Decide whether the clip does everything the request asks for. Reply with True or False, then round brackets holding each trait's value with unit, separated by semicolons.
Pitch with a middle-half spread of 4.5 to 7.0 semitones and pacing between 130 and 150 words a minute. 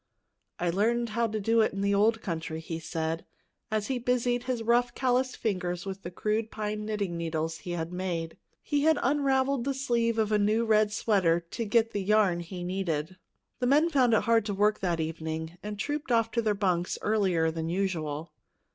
False (5.1 semitones; 200 wpm)